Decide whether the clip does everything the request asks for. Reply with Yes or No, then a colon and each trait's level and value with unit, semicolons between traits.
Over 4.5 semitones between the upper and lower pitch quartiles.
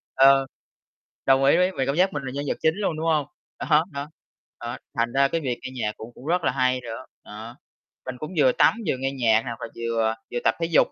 No: average, 4.0 semitones